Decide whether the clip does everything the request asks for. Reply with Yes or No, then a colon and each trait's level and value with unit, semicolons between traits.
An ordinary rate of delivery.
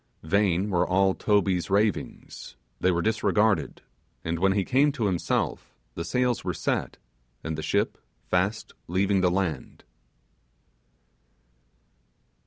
No: slow, 120 wpm